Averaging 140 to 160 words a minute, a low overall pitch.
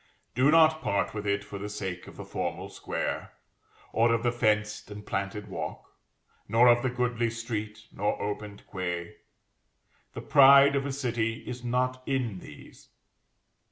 Yes: average, 155 wpm; low, 115 Hz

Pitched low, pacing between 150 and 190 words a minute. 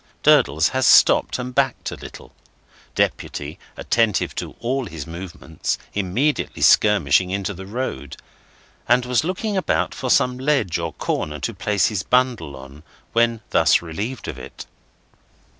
No: low, 105 Hz; average, 140 wpm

